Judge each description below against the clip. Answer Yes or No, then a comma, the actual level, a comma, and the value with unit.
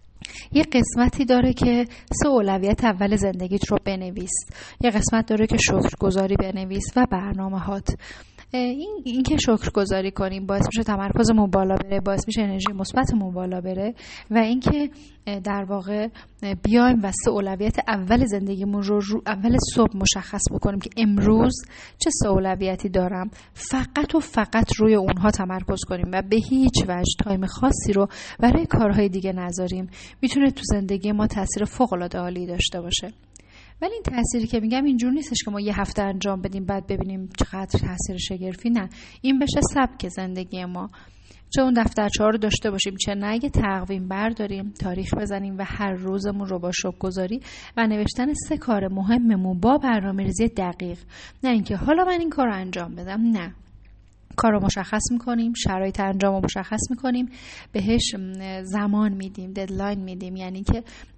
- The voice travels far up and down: No, average, 3.3 semitones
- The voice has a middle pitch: No, high, 205 Hz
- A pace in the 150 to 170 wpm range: Yes, fast, 155 wpm